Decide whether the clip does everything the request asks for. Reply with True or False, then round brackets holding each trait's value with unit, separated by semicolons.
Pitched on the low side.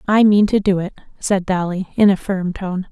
False (190 Hz)